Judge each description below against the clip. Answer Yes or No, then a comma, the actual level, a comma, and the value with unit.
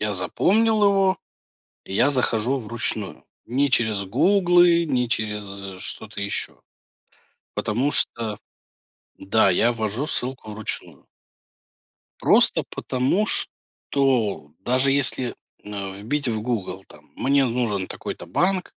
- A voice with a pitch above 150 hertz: No, low, 120 Hz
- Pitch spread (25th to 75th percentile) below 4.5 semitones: No, average, 5.2 semitones